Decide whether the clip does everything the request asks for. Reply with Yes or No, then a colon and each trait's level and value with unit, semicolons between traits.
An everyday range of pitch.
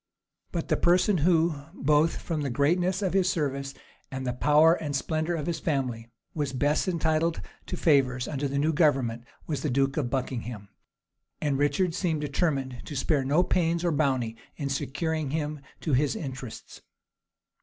Yes: average, 3.4 semitones